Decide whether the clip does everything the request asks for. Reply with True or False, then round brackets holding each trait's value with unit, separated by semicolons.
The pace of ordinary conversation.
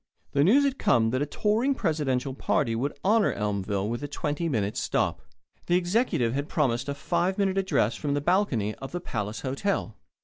True (190 wpm)